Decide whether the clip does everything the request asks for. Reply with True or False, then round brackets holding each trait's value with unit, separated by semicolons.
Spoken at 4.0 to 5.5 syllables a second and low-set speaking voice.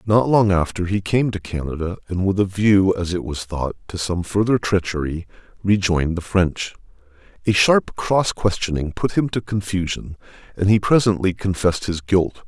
True (5.0 syllables/s; 95 Hz)